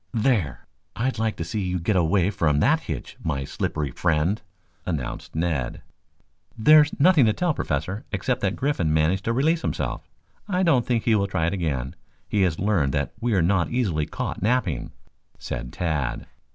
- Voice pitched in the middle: No, very low, 95 Hz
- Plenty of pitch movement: Yes, wide, 6.6 semitones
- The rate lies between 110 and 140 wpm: No, average, 175 wpm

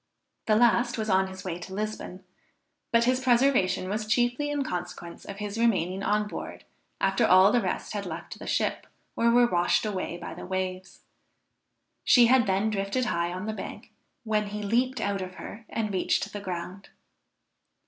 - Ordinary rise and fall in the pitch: Yes, average, 3.9 semitones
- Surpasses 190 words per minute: No, average, 180 wpm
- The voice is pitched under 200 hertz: No, high, 205 Hz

